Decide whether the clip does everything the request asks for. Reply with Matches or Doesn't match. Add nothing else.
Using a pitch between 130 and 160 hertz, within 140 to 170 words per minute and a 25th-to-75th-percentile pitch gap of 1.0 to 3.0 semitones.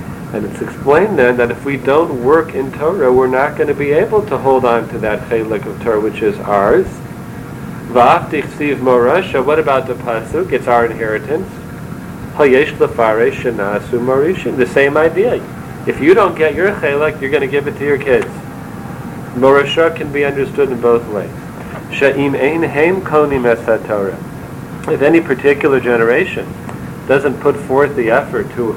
Doesn't match